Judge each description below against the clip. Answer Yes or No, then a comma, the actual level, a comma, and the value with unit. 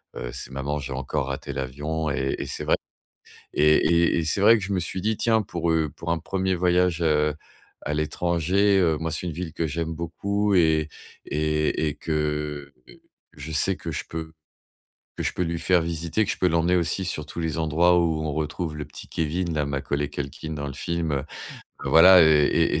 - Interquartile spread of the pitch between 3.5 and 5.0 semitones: No, narrow, 2.6 semitones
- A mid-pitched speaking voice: No, very low, 80 Hz